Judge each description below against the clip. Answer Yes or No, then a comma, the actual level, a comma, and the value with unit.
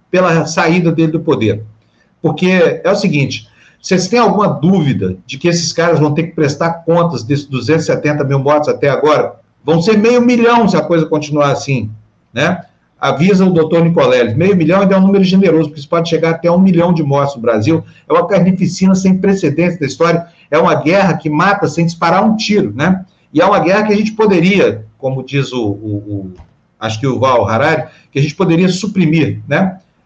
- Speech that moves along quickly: Yes, fast, 200 wpm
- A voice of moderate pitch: Yes, medium, 165 Hz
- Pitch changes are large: No, average, 4.8 semitones